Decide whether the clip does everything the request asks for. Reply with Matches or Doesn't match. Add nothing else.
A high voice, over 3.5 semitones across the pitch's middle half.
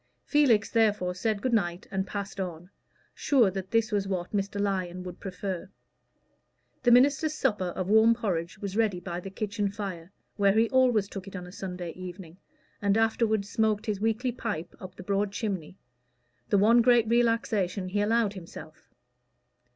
Doesn't match